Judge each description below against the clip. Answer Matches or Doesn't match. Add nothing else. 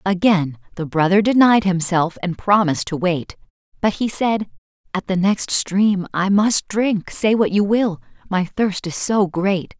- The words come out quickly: Doesn't match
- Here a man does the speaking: Doesn't match